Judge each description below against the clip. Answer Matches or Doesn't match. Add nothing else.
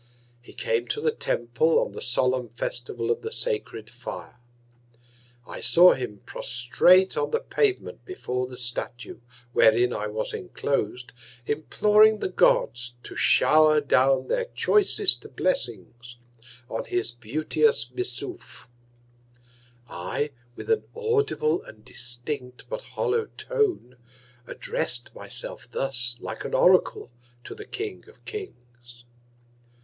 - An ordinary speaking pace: Doesn't match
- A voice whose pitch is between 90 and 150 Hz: Matches